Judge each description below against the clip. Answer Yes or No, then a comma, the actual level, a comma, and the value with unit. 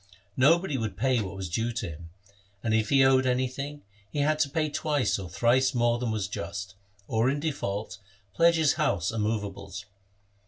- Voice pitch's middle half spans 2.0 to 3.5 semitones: No, wide, 5.5 semitones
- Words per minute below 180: No, average, 190 wpm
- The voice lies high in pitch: No, low, 120 Hz